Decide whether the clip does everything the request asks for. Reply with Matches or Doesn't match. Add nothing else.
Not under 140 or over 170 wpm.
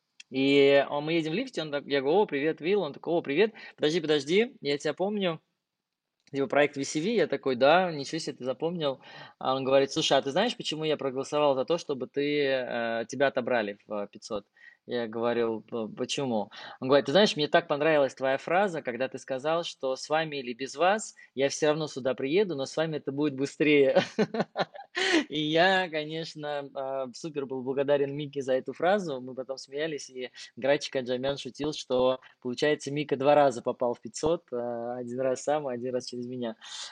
Doesn't match